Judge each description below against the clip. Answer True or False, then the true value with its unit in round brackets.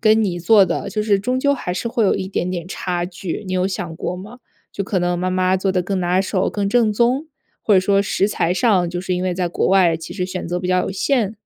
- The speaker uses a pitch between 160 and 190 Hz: True (185 Hz)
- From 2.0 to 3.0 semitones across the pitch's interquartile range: True (2.5 semitones)